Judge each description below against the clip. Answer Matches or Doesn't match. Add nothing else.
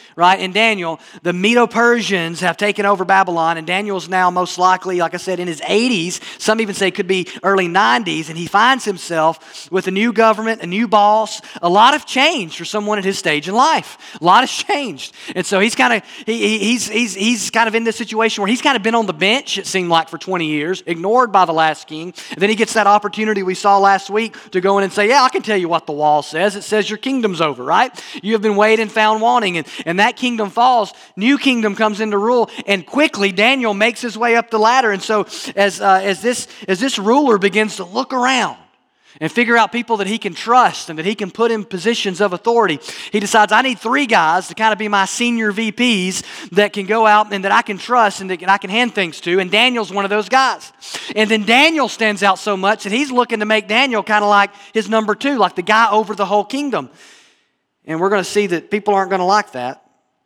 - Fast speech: Matches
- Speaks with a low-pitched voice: Doesn't match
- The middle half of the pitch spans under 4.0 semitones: Matches